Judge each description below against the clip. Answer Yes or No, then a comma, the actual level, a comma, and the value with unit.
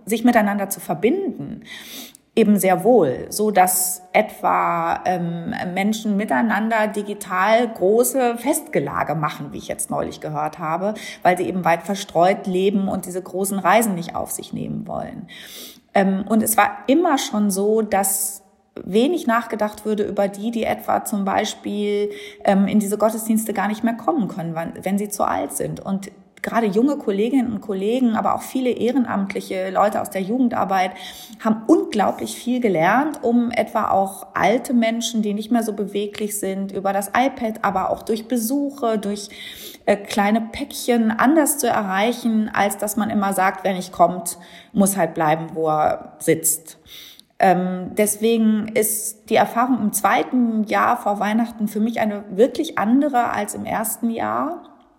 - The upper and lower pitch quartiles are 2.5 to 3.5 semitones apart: Yes, average, 3.0 semitones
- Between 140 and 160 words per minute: Yes, average, 155 wpm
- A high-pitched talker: Yes, high, 210 Hz